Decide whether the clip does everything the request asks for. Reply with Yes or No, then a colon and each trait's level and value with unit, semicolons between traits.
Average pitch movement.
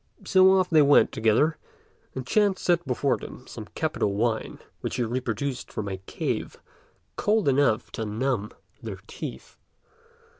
No: wide, 6.8 semitones